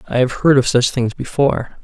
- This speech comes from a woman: No, male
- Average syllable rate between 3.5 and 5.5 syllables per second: No, 5.8 syllables/s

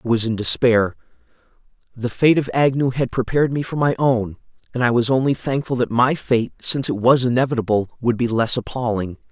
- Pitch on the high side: No, low, 125 Hz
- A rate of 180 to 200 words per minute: Yes, average, 195 wpm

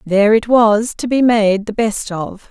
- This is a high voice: Yes, high, 215 Hz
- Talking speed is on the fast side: Yes, fast, 215 wpm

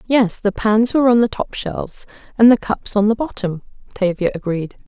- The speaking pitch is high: Yes, high, 215 Hz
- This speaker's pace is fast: No, average, 195 wpm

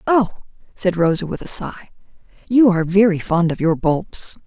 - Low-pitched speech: No, medium, 185 Hz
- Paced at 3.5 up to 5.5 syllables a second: Yes, 4.9 syllables/s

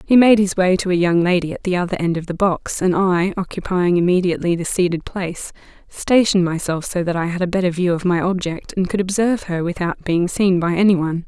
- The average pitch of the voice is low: No, medium, 180 Hz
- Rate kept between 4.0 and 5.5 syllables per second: No, 6.0 syllables/s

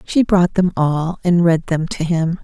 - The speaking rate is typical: No, fast, 220 wpm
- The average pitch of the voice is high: No, medium, 170 Hz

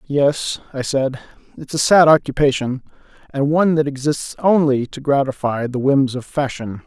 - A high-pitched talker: No, medium, 140 Hz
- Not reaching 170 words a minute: Yes, average, 155 wpm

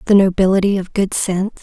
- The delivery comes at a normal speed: Yes, average, 185 wpm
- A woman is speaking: Yes, female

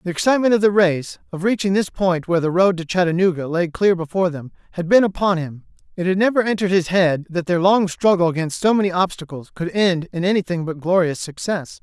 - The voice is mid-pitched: Yes, medium, 180 Hz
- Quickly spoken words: Yes, fast, 220 wpm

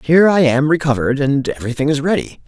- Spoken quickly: No, average, 195 wpm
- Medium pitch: Yes, medium, 145 Hz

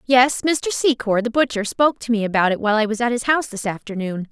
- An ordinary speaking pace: No, fast, 250 wpm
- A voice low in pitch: No, high, 235 Hz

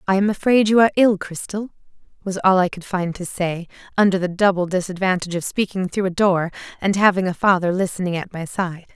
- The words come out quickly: Yes, fast, 210 wpm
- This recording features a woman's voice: Yes, female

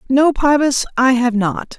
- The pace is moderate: Yes, average, 170 wpm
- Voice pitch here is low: No, very high, 255 Hz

